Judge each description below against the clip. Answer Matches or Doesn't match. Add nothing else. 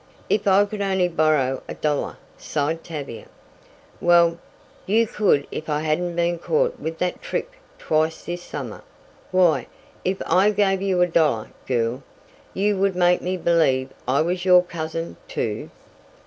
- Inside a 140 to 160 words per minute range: Matches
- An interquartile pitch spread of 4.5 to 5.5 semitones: Doesn't match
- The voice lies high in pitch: Doesn't match